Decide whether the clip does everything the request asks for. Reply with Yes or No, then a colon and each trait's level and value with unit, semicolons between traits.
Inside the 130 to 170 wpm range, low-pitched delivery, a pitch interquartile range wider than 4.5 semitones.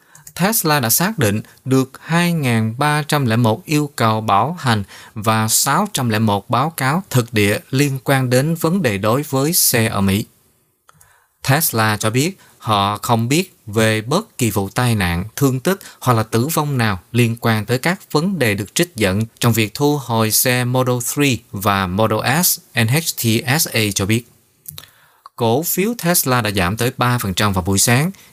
Yes: slow, 165 wpm; low, 120 Hz; average, 5.2 semitones